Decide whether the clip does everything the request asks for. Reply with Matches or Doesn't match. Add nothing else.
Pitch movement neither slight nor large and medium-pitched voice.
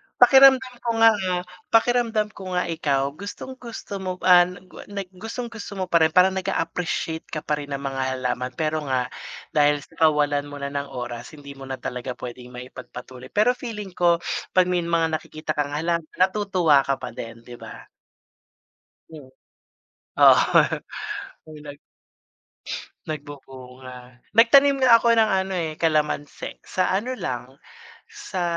Doesn't match